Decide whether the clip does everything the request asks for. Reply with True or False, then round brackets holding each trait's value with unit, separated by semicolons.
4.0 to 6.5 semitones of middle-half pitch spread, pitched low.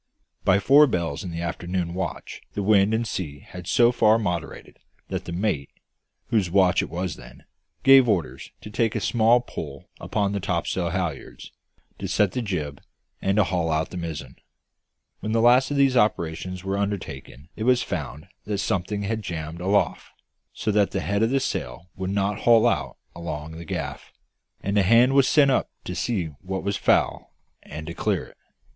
True (4.3 semitones; 95 Hz)